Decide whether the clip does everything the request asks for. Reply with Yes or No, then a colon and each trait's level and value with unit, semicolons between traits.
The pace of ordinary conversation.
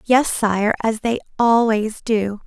Yes: average, 145 wpm